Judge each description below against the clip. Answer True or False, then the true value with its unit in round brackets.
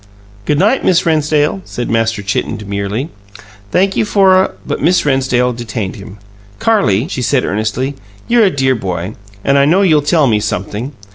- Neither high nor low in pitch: False (130 Hz)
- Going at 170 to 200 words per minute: True (180 wpm)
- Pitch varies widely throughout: True (7.6 semitones)